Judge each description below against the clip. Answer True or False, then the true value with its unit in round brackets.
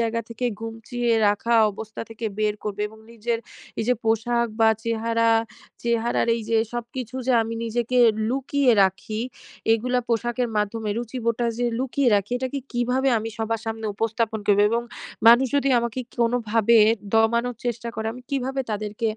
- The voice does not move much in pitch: True (1.6 semitones)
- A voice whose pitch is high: True (230 Hz)